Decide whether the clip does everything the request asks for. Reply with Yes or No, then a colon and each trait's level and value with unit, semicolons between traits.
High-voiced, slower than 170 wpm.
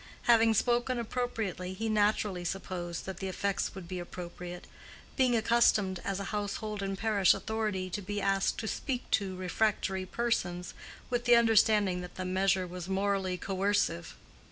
Yes: high, 195 Hz; average, 155 wpm